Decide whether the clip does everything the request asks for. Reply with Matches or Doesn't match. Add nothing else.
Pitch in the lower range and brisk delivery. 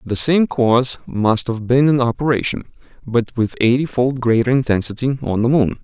Doesn't match